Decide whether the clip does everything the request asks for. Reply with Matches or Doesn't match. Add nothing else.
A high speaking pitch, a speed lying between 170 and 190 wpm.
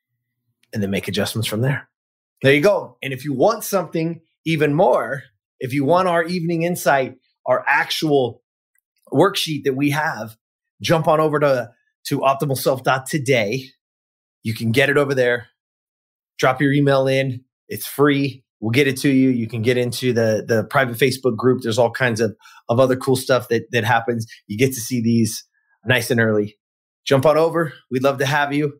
Doesn't match